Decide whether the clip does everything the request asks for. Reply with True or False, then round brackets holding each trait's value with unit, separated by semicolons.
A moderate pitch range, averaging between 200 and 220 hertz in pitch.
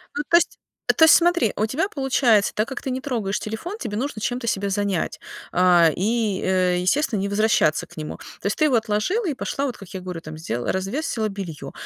False (6.0 semitones; 215 Hz)